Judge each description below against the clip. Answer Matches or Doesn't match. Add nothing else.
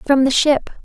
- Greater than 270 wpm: Doesn't match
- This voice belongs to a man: Doesn't match